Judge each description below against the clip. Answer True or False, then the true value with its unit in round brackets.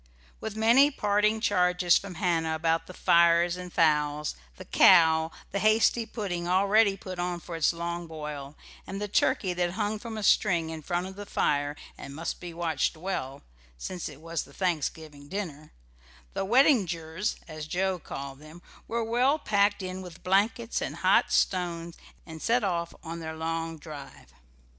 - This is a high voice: False (175 Hz)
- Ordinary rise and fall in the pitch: True (3.8 semitones)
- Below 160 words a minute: False (165 wpm)